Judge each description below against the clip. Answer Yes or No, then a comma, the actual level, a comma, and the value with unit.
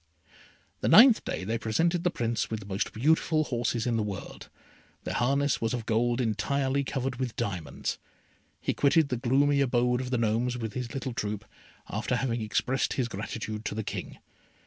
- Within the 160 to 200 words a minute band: Yes, average, 180 wpm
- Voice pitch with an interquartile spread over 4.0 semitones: No, average, 3.3 semitones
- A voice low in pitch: Yes, low, 120 Hz